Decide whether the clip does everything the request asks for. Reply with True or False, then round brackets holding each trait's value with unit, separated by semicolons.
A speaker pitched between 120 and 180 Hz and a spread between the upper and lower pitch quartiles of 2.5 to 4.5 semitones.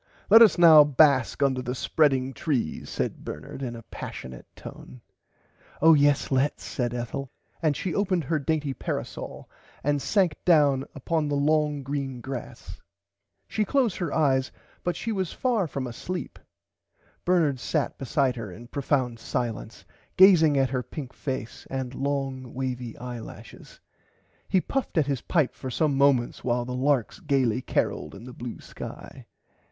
True (140 Hz; 3.6 semitones)